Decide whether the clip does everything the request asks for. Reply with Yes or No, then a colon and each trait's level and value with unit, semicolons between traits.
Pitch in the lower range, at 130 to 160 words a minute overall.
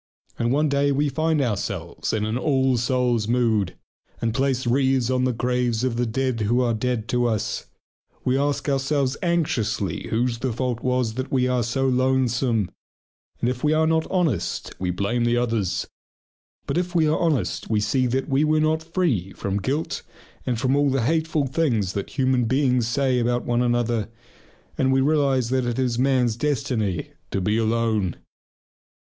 No: low, 125 Hz; average, 175 wpm